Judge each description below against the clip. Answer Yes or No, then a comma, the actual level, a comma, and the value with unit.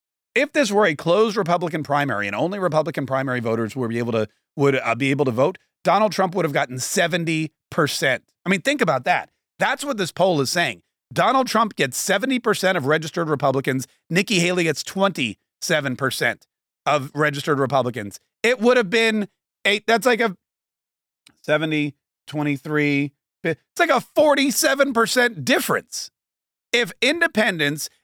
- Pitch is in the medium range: Yes, medium, 170 Hz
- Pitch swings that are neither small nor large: No, wide, 7.3 semitones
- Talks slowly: No, average, 150 wpm